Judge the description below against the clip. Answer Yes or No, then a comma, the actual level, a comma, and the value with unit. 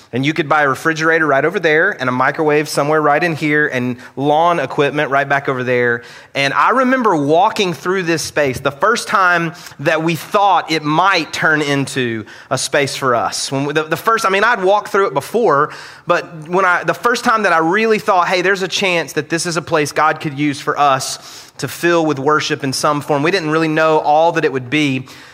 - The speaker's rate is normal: No, fast, 225 wpm